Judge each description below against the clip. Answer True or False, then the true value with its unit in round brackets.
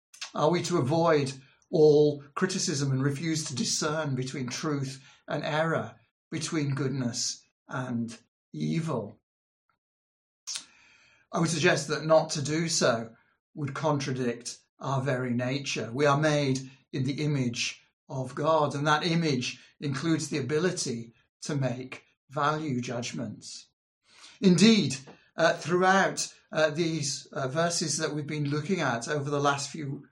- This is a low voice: False (145 Hz)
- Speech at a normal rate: False (130 wpm)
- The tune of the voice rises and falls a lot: False (3.4 semitones)